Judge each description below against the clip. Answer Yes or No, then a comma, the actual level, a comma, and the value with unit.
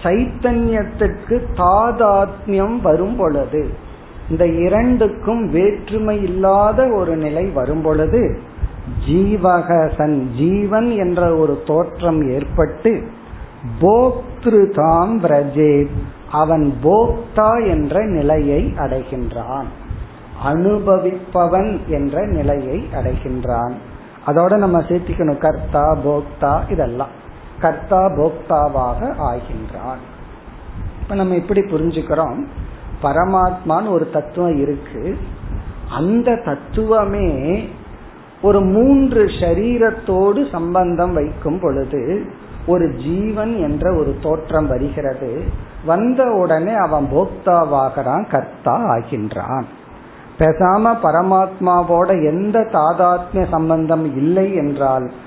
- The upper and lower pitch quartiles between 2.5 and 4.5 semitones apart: No, average, 5.3 semitones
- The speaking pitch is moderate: Yes, medium, 170 Hz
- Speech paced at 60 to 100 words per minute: Yes, slow, 75 wpm